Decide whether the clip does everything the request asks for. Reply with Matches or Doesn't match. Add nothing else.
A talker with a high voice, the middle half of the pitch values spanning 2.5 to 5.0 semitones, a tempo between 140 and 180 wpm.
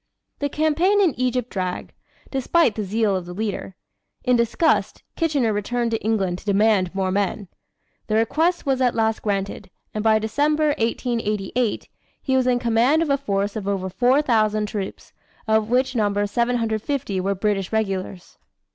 Matches